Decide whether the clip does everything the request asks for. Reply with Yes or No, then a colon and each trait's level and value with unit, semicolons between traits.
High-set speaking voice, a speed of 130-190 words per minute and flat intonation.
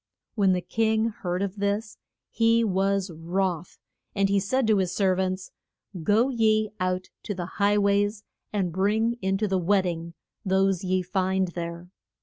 Yes: high, 195 Hz; average, 165 wpm; narrow, 2.1 semitones